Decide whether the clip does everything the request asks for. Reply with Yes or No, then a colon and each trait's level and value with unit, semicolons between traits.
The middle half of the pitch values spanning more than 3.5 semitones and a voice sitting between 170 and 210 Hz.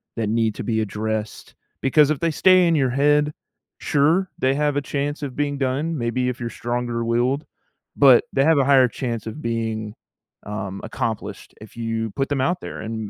No: average, 4.3 semitones; low, 130 Hz